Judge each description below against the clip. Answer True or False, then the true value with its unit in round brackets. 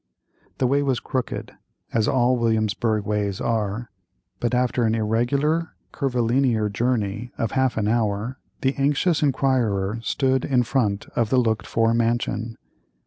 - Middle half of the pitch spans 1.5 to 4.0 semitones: True (3.1 semitones)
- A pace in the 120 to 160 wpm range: True (140 wpm)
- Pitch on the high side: False (120 Hz)